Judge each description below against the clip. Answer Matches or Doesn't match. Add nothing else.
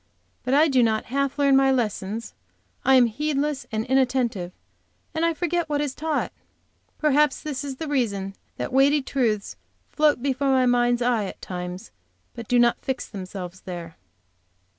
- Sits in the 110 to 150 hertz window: Doesn't match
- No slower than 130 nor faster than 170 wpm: Matches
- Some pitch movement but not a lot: Matches